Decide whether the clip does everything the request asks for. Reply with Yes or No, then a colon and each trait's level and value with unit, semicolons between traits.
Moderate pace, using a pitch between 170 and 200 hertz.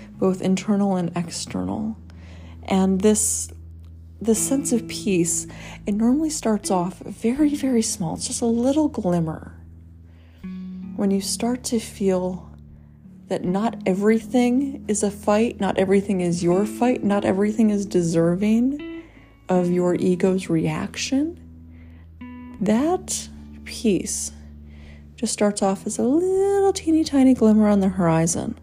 No: slow, 125 wpm; high, 190 Hz